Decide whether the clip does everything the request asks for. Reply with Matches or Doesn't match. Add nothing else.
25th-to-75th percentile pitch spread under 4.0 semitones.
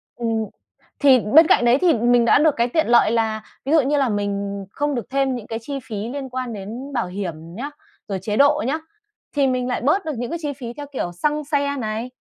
Doesn't match